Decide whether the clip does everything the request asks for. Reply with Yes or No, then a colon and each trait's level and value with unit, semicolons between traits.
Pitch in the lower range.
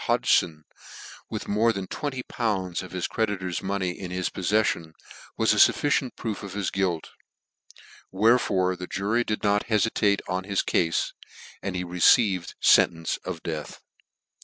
Yes: very low, 95 Hz